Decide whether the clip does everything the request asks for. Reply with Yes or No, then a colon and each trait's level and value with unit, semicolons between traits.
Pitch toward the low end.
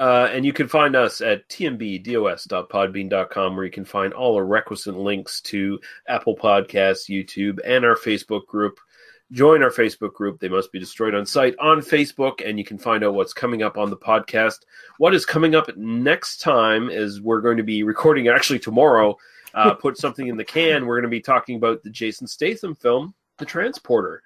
Yes: low, 110 Hz